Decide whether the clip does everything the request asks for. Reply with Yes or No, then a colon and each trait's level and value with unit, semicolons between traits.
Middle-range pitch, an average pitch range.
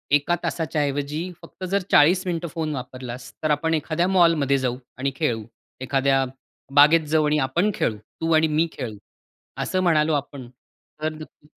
Yes: medium, 150 Hz; average, 3.2 semitones